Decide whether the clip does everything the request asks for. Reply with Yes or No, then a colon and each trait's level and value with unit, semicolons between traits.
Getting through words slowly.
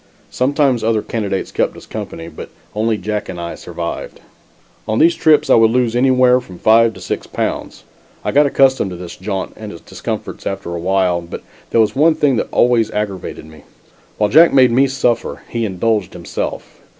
No: average, 185 wpm